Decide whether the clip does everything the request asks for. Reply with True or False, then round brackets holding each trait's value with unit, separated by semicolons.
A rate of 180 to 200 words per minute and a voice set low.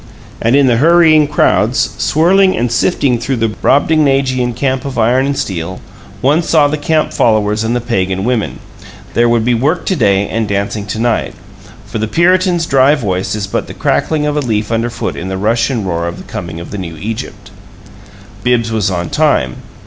True (195 wpm; 120 Hz)